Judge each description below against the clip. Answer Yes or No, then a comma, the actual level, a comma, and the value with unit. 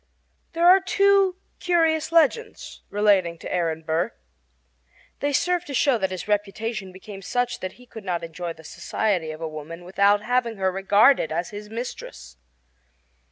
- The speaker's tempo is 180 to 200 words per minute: No, average, 160 wpm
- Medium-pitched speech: No, high, 205 Hz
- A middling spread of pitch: No, wide, 6.8 semitones